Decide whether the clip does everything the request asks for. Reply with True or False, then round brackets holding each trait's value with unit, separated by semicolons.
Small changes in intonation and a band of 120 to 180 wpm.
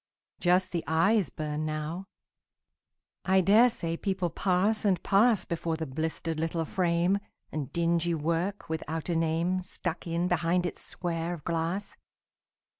True (2.3 semitones; 140 wpm)